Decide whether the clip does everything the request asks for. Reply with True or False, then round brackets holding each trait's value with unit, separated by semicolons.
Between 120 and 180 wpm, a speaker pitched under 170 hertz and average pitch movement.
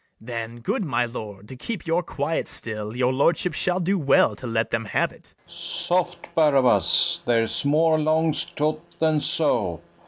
False (165 wpm; 140 Hz; 5.7 semitones)